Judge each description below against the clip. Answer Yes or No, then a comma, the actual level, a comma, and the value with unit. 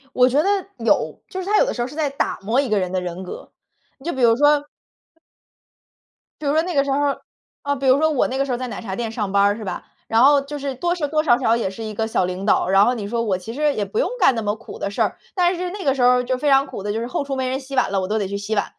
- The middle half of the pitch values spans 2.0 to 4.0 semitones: No, average, 5.2 semitones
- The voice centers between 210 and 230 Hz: No, very high, 255 Hz